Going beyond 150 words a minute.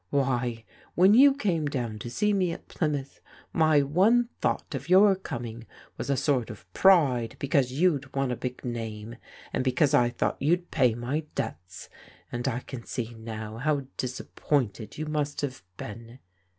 Yes: average, 165 wpm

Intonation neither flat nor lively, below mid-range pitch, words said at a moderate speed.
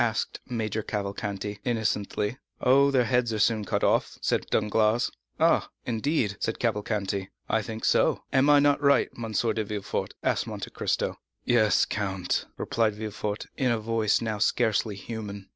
No: narrow, 2.3 semitones; low, 110 Hz; average, 155 wpm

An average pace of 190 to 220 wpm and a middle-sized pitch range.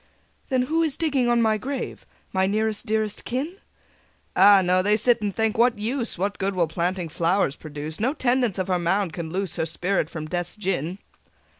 Yes: average, 195 wpm; average, 5.0 semitones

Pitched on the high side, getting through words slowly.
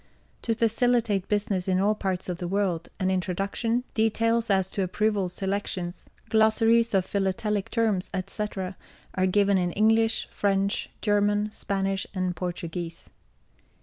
Yes: high, 200 Hz; slow, 130 wpm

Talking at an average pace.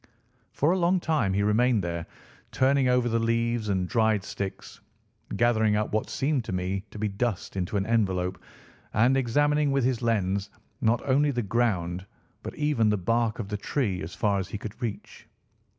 Yes: average, 180 wpm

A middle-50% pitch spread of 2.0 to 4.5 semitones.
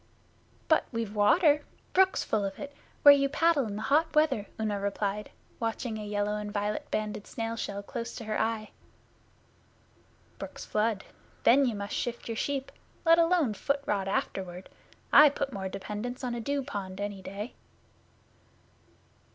No: average, 5.2 semitones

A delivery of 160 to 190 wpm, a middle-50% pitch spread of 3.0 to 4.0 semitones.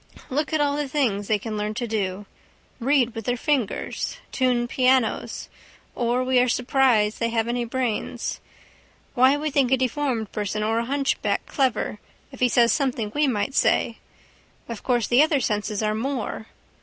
Yes: average, 170 wpm; average, 3.5 semitones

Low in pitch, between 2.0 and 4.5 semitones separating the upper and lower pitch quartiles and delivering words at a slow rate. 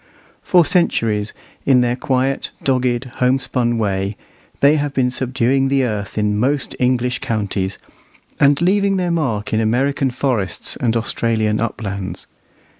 Yes: low, 125 Hz; average, 4.0 semitones; slow, 130 wpm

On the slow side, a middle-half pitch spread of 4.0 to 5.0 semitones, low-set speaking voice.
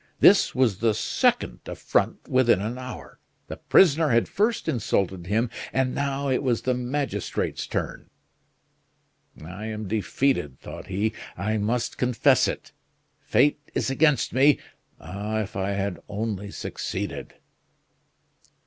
Yes: slow, 130 wpm; average, 4.5 semitones; low, 115 Hz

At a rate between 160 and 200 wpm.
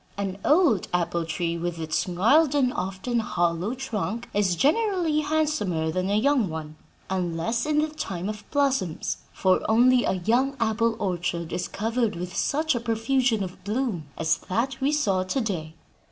Yes: average, 165 wpm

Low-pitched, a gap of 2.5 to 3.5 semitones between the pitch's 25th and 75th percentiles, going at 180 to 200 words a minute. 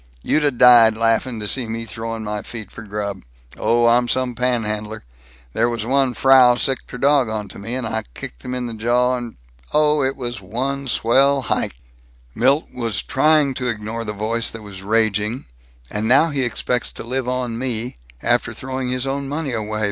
Yes: low, 120 Hz; average, 2.9 semitones; average, 190 wpm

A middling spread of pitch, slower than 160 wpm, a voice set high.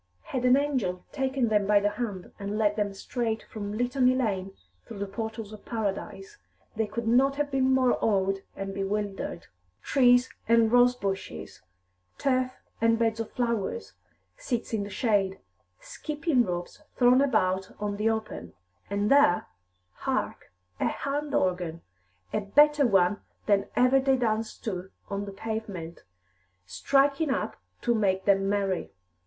Yes: average, 4.2 semitones; average, 150 wpm; high, 220 Hz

